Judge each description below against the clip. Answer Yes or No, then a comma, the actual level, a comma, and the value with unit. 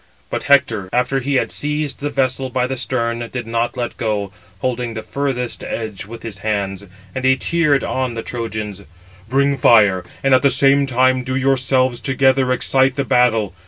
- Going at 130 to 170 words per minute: No, average, 185 wpm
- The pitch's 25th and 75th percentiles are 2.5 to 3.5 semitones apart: Yes, average, 2.8 semitones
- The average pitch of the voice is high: No, low, 125 Hz